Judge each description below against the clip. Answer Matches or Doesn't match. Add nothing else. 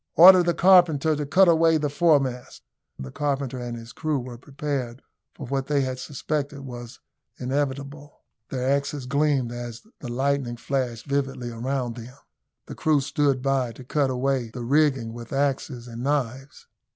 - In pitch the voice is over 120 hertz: Matches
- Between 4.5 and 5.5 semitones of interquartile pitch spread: Doesn't match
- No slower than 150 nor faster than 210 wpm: Matches